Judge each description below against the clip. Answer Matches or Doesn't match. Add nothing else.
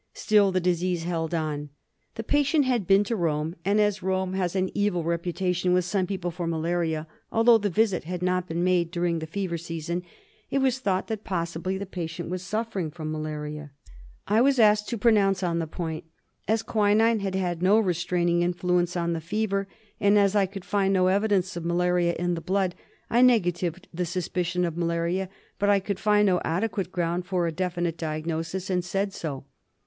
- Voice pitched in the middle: Matches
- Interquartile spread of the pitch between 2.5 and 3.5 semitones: Matches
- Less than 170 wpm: Doesn't match